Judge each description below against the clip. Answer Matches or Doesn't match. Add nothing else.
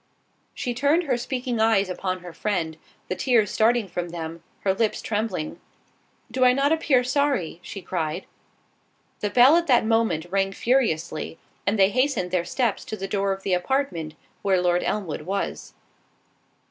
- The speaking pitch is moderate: Doesn't match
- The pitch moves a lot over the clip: Matches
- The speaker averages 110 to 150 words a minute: Doesn't match